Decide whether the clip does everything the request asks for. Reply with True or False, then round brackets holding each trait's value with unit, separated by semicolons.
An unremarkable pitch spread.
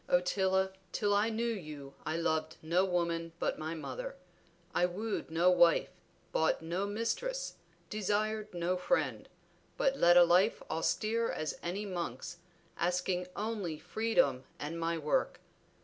True (4.2 semitones)